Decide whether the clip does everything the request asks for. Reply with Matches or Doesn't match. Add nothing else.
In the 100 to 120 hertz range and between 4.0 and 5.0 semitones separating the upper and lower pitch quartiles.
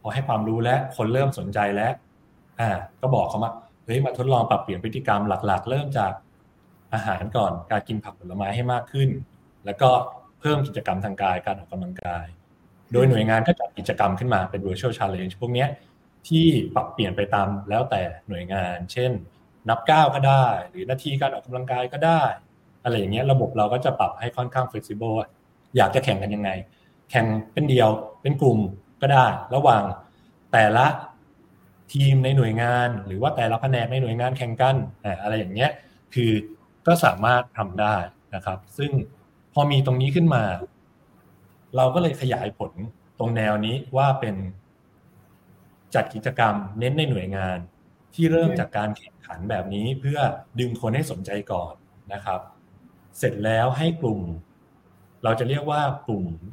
Matches